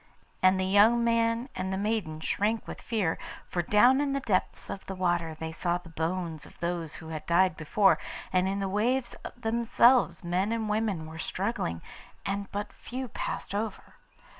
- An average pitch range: Yes, average, 4.7 semitones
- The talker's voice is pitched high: Yes, high, 195 Hz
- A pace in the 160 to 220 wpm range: Yes, average, 180 wpm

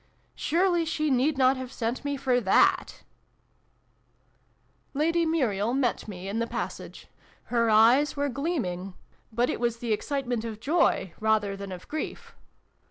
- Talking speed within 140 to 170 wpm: Yes, average, 165 wpm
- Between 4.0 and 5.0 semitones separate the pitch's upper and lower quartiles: Yes, average, 4.7 semitones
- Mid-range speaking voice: No, high, 245 Hz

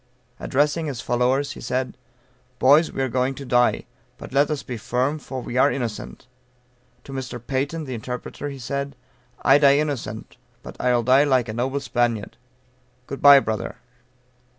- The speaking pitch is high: No, low, 130 Hz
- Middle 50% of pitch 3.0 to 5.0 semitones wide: No, narrow, 2.4 semitones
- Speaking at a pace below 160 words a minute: No, average, 165 wpm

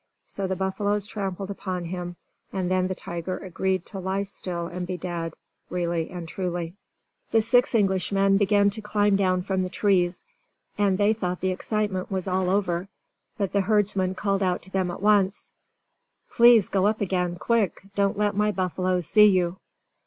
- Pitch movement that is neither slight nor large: No, narrow, 2.0 semitones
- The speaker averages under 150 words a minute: No, average, 175 wpm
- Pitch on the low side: No, high, 190 Hz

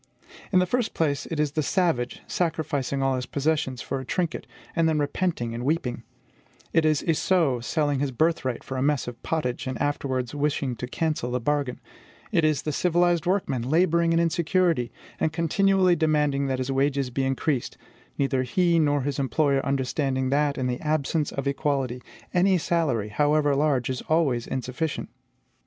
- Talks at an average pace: Yes, average, 170 wpm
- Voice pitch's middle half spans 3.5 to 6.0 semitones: Yes, average, 3.8 semitones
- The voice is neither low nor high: Yes, medium, 145 Hz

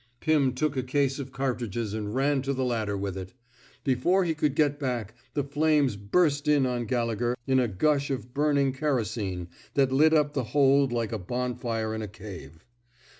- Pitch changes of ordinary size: Yes, average, 4.3 semitones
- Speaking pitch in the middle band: No, low, 130 Hz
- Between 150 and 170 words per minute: No, average, 190 wpm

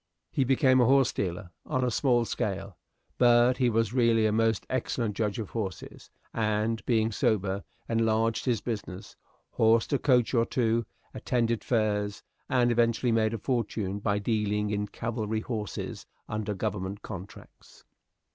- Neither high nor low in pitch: No, low, 110 Hz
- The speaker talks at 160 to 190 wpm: No, average, 145 wpm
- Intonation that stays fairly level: Yes, narrow, 2.3 semitones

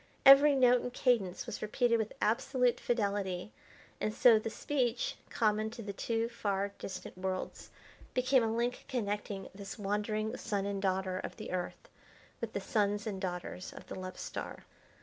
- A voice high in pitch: Yes, high, 215 Hz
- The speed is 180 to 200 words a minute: No, average, 165 wpm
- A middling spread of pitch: Yes, average, 3.5 semitones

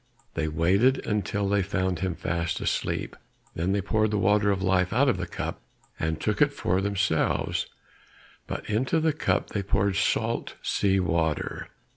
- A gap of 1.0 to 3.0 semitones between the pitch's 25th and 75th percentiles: Yes, narrow, 2.4 semitones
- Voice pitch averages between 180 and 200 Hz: No, very low, 95 Hz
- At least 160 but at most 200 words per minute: Yes, average, 165 wpm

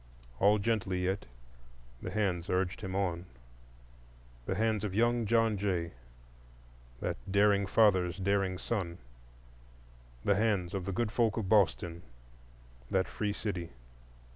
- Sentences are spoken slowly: Yes, slow, 120 wpm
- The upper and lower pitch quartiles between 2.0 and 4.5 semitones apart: Yes, average, 3.2 semitones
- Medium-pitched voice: No, very low, 95 Hz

